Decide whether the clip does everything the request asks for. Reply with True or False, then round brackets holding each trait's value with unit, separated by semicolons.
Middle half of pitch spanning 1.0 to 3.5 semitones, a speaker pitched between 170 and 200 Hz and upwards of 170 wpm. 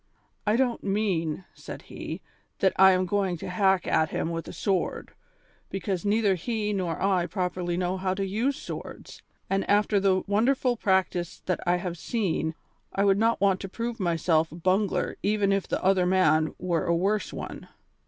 True (2.5 semitones; 190 Hz; 180 wpm)